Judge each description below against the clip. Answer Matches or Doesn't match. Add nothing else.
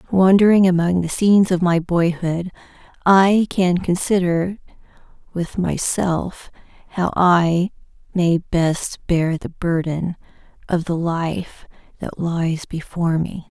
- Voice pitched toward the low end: Doesn't match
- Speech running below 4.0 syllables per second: Matches